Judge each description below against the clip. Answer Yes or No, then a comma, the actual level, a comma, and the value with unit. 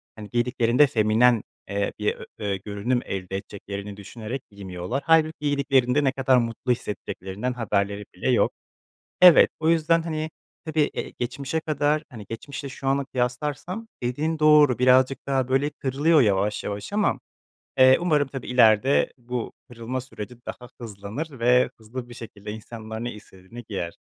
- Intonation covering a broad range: No, average, 4.8 semitones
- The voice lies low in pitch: Yes, low, 125 Hz